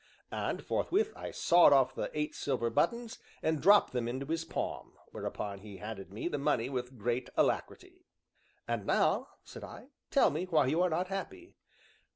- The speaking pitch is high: No, medium, 150 Hz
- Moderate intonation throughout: No, wide, 7.0 semitones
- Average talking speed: Yes, average, 175 wpm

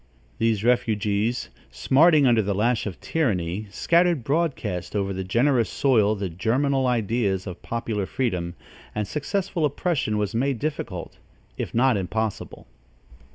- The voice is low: Yes, low, 115 Hz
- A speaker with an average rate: No, slow, 130 wpm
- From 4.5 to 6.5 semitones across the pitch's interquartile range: Yes, average, 5.1 semitones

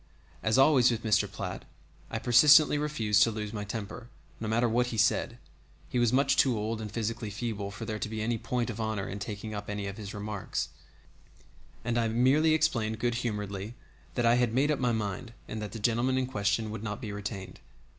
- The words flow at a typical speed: No, fast, 210 wpm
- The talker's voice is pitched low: Yes, low, 110 Hz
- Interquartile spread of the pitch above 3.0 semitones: No, average, 2.7 semitones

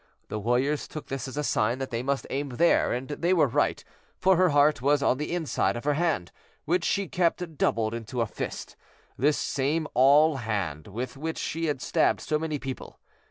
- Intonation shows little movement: No, average, 4.4 semitones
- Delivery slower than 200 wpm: No, fast, 205 wpm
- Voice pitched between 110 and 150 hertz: Yes, medium, 140 Hz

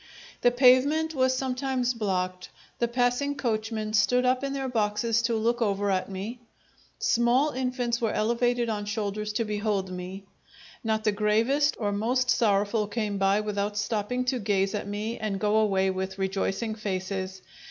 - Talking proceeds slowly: No, average, 160 wpm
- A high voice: Yes, high, 220 Hz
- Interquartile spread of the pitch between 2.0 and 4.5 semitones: Yes, average, 3.4 semitones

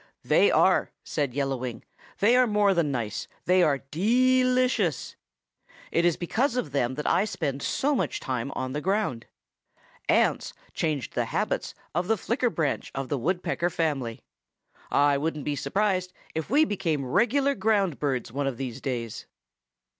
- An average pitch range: No, wide, 7.3 semitones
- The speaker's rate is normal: Yes, average, 165 wpm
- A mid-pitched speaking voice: Yes, medium, 160 Hz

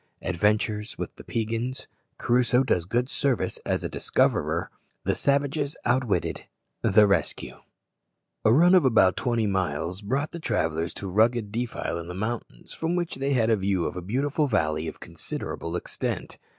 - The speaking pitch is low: Yes, low, 110 Hz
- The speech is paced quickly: No, average, 160 wpm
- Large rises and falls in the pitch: Yes, wide, 5.8 semitones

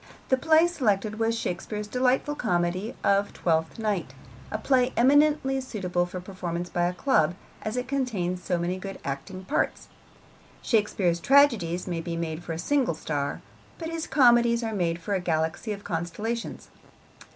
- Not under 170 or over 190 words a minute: No, average, 160 wpm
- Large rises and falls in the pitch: Yes, wide, 6.2 semitones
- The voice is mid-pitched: No, high, 200 Hz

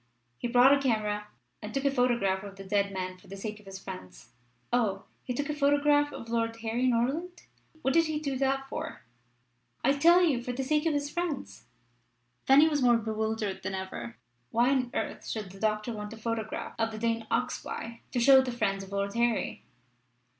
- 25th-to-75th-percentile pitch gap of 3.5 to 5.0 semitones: Yes, average, 4.6 semitones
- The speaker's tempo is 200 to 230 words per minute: Yes, fast, 205 wpm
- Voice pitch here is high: Yes, high, 235 Hz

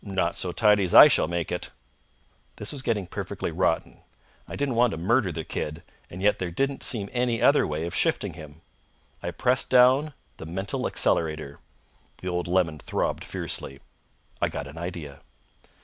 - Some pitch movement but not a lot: No, wide, 6.1 semitones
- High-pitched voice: No, very low, 90 Hz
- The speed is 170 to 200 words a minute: Yes, average, 175 wpm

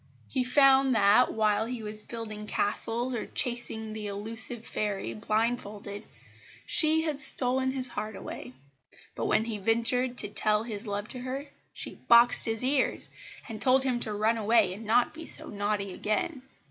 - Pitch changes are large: No, average, 3.1 semitones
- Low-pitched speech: No, high, 225 Hz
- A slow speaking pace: No, average, 165 wpm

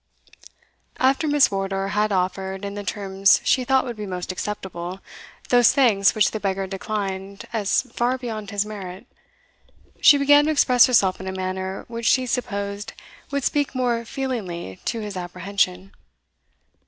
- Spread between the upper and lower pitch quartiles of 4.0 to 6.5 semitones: Yes, average, 4.3 semitones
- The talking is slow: No, average, 155 wpm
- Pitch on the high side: Yes, high, 205 Hz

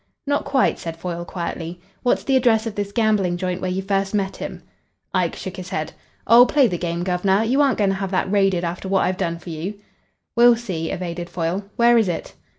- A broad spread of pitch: No, average, 3.8 semitones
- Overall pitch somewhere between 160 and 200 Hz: Yes, high, 190 Hz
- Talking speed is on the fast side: Yes, fast, 220 wpm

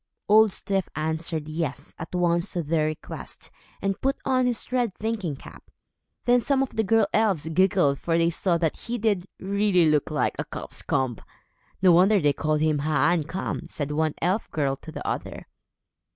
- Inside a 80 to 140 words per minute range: No, average, 185 wpm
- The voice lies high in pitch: No, medium, 175 Hz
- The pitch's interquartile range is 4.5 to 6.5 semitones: Yes, average, 5.0 semitones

